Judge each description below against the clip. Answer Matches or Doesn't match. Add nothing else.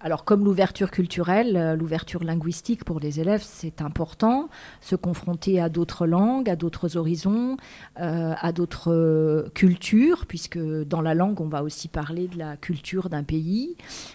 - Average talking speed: Matches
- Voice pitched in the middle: Matches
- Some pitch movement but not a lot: Matches